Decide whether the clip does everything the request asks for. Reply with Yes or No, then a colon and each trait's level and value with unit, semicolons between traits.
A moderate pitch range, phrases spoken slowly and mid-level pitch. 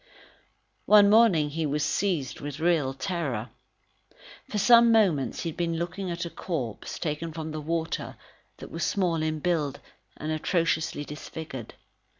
No: average, 3.0 semitones; average, 150 wpm; medium, 165 Hz